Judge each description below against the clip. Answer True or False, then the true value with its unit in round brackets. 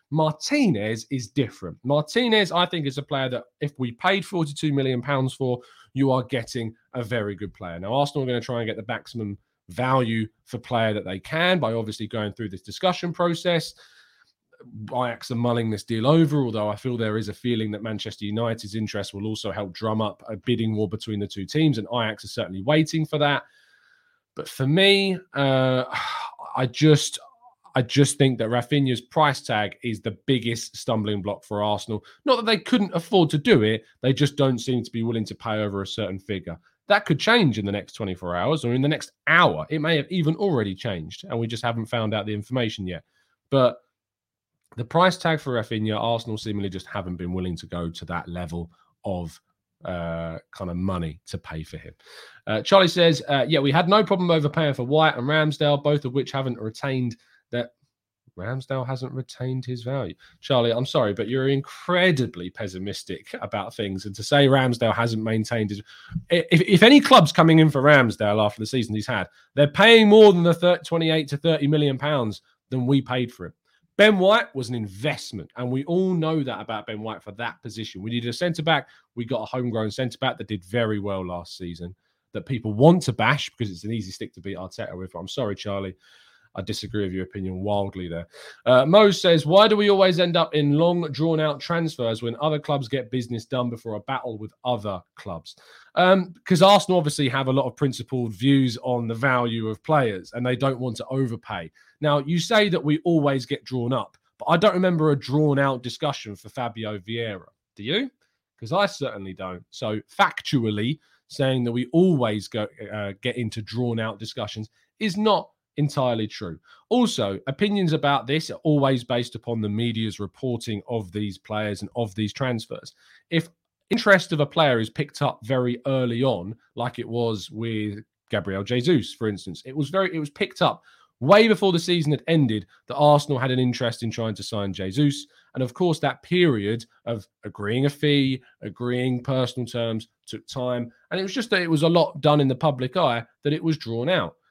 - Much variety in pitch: True (5.9 semitones)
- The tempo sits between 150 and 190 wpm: False (200 wpm)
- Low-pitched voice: True (125 Hz)